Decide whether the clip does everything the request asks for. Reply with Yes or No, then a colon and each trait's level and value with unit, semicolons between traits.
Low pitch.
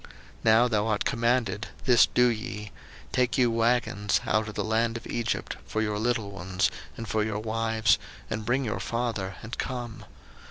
Yes: low, 110 Hz